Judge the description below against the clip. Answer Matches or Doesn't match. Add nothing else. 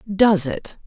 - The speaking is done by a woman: Matches